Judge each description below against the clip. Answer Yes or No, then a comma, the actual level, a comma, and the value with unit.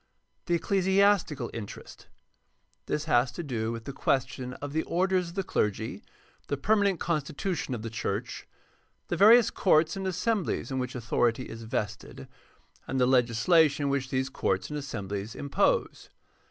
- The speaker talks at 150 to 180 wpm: Yes, average, 155 wpm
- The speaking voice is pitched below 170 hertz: Yes, medium, 140 Hz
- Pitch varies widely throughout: Yes, wide, 6.7 semitones